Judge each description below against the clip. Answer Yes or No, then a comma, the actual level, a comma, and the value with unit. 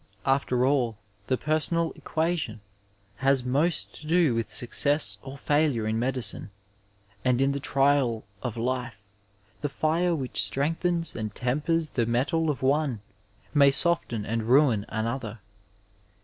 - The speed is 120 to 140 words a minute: Yes, slow, 135 wpm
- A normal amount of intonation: Yes, average, 4.5 semitones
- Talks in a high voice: No, low, 135 Hz